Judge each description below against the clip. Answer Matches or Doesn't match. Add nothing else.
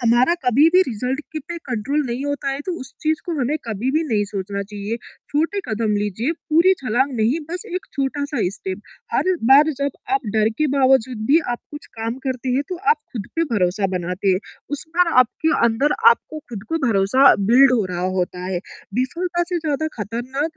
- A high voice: Matches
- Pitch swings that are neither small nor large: Doesn't match